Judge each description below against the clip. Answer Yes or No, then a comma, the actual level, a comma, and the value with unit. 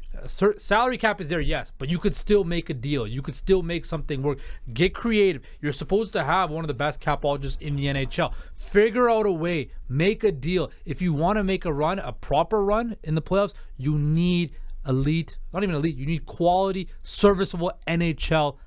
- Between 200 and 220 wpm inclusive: Yes, fast, 205 wpm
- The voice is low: No, medium, 170 Hz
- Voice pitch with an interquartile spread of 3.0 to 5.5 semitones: Yes, average, 4.8 semitones